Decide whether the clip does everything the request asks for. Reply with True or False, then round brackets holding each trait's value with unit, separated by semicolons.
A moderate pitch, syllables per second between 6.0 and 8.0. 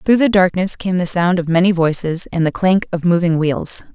False (175 Hz; 5.1 syllables/s)